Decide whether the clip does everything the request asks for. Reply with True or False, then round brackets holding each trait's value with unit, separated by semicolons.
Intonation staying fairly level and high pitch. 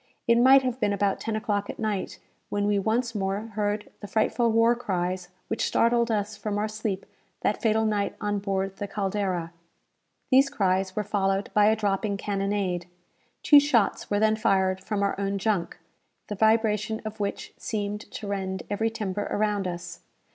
True (2.0 semitones; 205 Hz)